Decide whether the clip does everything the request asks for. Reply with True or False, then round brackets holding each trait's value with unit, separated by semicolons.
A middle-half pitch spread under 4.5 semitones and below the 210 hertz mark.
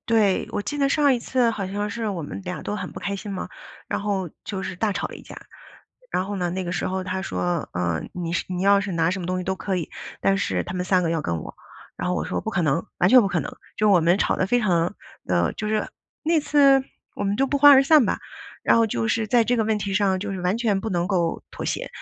True (3.5 semitones; 195 Hz)